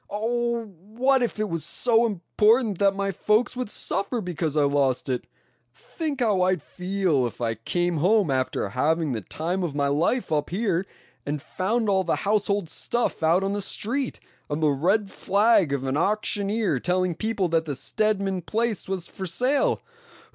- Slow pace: No, average, 175 wpm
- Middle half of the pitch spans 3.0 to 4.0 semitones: No, average, 5.3 semitones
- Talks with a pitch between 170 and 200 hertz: Yes, high, 190 Hz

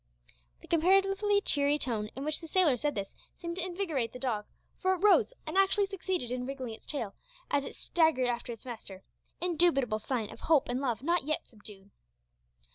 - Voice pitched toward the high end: Yes, very high, 285 Hz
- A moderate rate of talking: Yes, average, 190 wpm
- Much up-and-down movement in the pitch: Yes, wide, 6.6 semitones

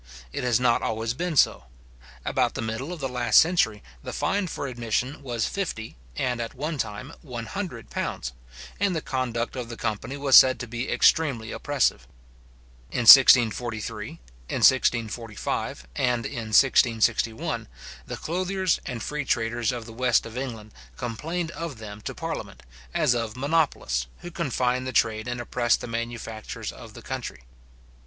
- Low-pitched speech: Yes, low, 120 Hz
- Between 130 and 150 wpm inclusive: No, average, 160 wpm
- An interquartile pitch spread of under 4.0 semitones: Yes, average, 3.6 semitones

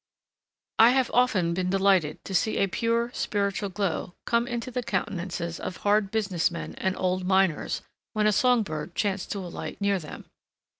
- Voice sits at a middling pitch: No, high, 195 Hz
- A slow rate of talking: No, average, 170 wpm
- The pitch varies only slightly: No, average, 3.4 semitones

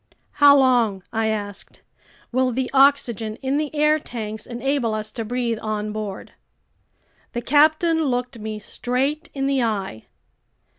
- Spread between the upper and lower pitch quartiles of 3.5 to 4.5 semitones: Yes, average, 4.2 semitones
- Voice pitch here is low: No, high, 245 Hz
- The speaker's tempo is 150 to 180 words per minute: No, average, 140 wpm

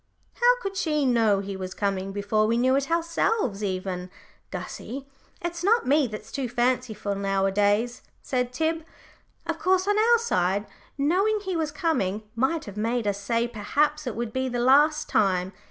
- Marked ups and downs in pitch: Yes, wide, 7.8 semitones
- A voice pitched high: Yes, high, 245 Hz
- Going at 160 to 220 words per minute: Yes, average, 170 wpm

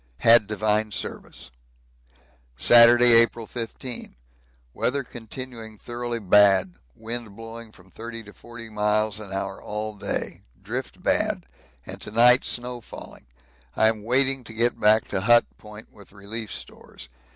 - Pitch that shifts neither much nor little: No, narrow, 2.0 semitones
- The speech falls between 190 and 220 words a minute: No, average, 140 wpm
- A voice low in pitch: Yes, low, 110 Hz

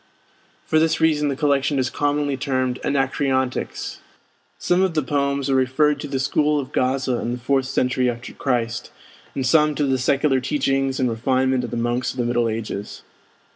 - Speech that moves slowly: No, average, 180 wpm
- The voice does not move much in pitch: Yes, narrow, 2.3 semitones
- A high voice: No, low, 135 Hz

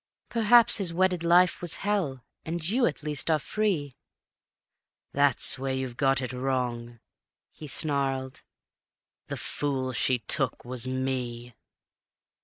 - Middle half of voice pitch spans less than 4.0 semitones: No, average, 4.7 semitones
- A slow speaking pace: Yes, slow, 130 wpm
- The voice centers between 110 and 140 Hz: Yes, low, 135 Hz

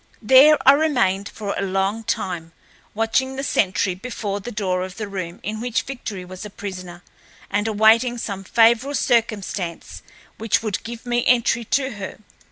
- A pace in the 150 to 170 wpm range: Yes, average, 165 wpm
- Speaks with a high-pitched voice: Yes, high, 215 Hz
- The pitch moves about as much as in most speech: Yes, average, 3.8 semitones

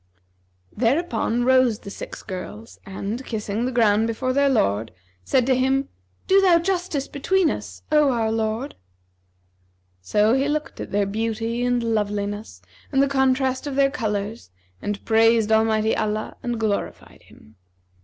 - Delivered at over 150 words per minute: No, average, 145 wpm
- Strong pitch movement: No, average, 4.0 semitones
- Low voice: No, high, 230 Hz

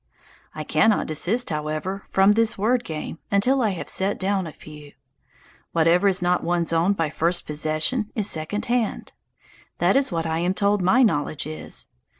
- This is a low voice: No, medium, 180 Hz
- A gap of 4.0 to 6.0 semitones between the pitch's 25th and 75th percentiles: Yes, average, 4.5 semitones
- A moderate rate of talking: Yes, average, 170 wpm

